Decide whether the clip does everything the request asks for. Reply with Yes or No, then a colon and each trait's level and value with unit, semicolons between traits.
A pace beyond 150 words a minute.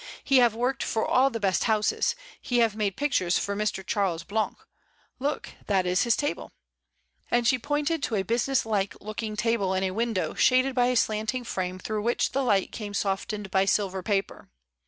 Yes: average, 200 wpm